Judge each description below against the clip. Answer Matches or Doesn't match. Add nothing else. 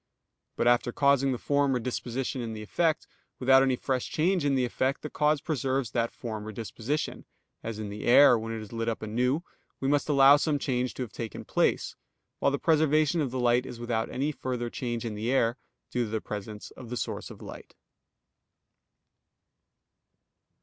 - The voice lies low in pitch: Matches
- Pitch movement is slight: Doesn't match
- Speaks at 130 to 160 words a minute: Doesn't match